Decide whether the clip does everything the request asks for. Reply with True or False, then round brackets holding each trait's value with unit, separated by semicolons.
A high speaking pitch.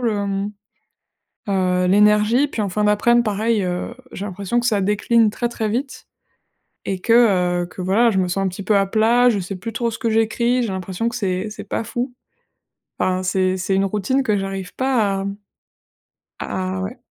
True (205 Hz)